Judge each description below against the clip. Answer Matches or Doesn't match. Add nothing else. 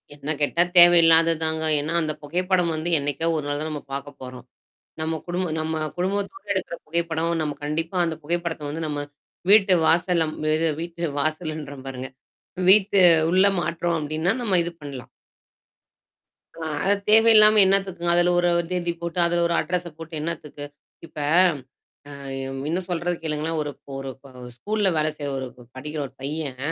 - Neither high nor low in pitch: Matches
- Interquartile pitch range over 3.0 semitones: Doesn't match